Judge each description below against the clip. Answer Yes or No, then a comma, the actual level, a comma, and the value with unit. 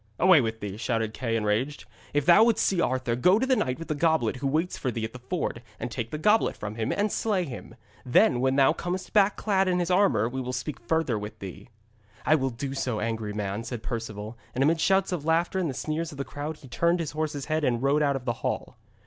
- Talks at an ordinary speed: No, fast, 250 wpm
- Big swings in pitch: Yes, wide, 6.3 semitones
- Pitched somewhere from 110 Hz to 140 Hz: Yes, low, 135 Hz